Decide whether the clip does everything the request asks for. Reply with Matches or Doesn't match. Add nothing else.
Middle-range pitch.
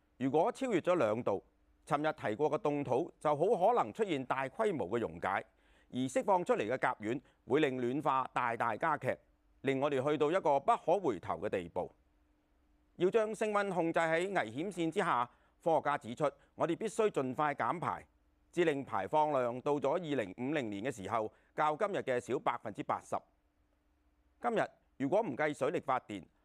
Matches